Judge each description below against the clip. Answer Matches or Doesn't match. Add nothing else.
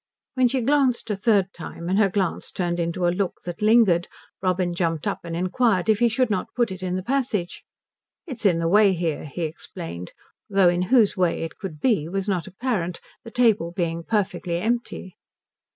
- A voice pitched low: Doesn't match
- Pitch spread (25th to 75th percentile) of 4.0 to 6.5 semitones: Matches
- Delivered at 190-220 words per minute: Matches